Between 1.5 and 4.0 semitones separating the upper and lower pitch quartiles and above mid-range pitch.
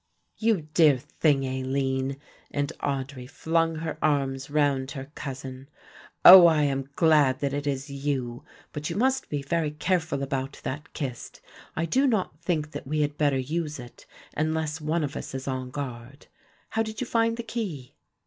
No: average, 3.3 semitones; medium, 145 Hz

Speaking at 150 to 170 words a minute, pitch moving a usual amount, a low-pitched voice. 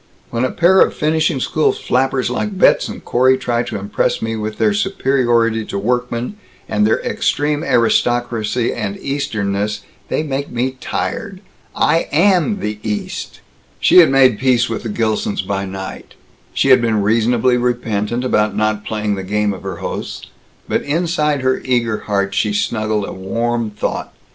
Yes: average, 165 wpm; average, 4.0 semitones; low, 120 Hz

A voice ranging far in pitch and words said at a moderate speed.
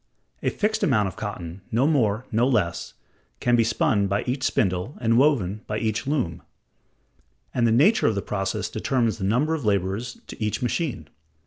No: average, 4.4 semitones; average, 180 wpm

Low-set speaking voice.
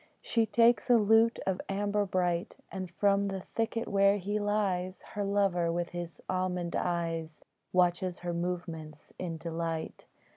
No: medium, 185 Hz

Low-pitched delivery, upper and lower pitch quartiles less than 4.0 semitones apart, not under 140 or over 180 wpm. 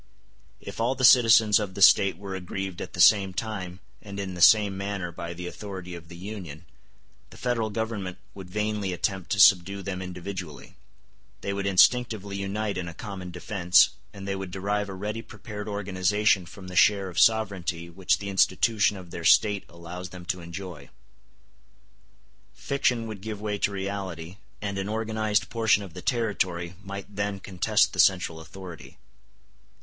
Yes: low, 100 Hz; narrow, 2.4 semitones; average, 170 wpm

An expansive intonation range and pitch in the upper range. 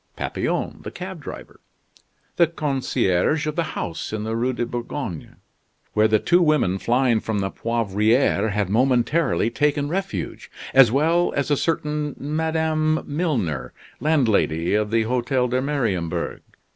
No: wide, 5.7 semitones; low, 130 Hz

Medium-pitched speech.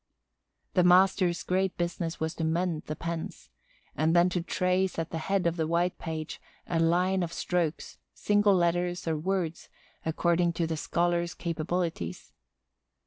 Yes: medium, 170 Hz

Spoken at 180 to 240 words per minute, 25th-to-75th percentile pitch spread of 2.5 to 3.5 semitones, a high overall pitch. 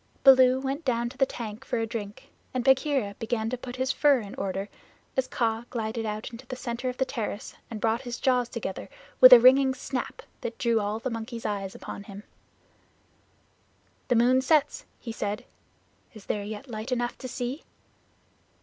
Yes: average, 185 wpm; average, 2.9 semitones; high, 240 Hz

